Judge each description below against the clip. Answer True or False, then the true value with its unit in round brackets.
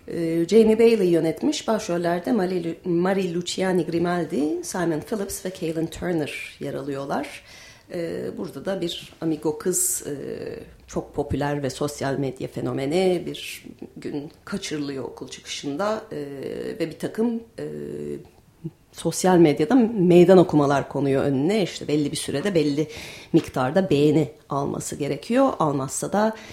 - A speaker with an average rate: True (125 wpm)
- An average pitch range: True (4.6 semitones)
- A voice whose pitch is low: False (165 Hz)